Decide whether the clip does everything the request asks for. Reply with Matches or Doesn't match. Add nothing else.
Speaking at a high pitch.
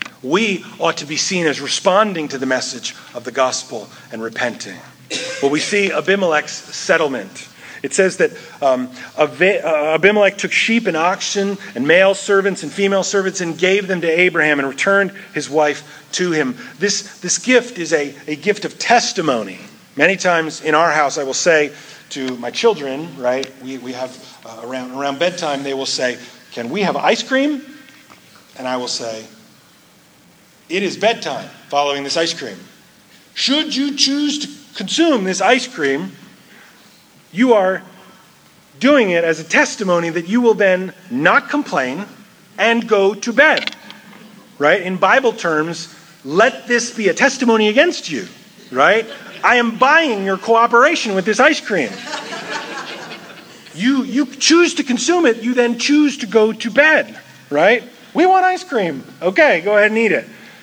Matches